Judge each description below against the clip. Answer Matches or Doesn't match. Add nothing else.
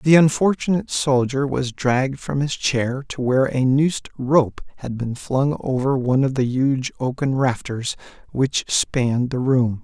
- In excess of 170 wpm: Doesn't match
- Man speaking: Matches